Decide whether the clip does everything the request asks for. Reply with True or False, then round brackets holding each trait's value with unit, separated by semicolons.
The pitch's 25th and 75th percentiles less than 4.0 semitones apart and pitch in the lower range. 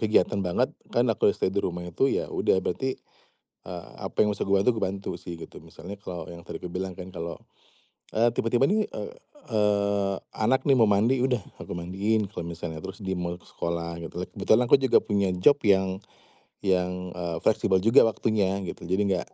True (3.4 semitones; 95 Hz)